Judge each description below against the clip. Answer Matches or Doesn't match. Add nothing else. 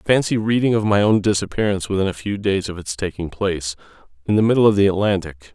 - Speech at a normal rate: Doesn't match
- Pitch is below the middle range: Matches